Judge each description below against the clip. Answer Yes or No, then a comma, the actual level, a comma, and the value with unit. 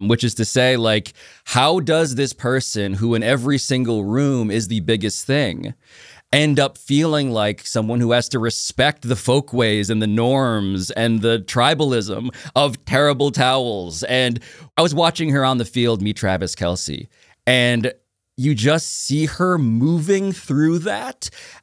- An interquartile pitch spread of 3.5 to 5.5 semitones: Yes, average, 4.2 semitones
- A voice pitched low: Yes, low, 125 Hz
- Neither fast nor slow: Yes, average, 160 wpm